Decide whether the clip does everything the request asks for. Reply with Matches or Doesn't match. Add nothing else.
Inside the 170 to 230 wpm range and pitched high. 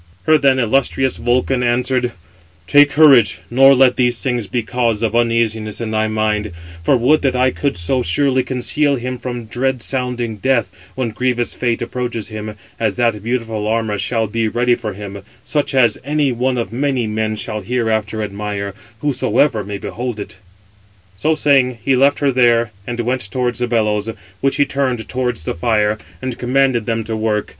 Doesn't match